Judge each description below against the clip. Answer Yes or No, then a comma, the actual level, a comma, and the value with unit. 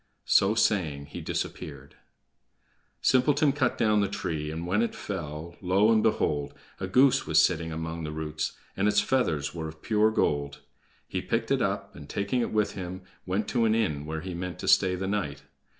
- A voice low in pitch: Yes, very low, 90 Hz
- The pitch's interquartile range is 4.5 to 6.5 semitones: Yes, wide, 5.4 semitones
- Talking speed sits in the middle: Yes, average, 190 wpm